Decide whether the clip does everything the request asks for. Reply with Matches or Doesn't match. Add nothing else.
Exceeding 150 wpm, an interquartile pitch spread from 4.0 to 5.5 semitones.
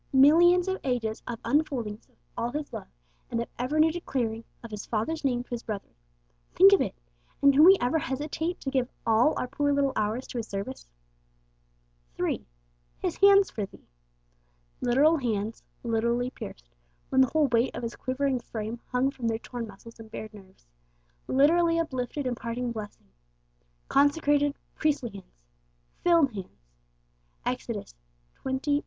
Matches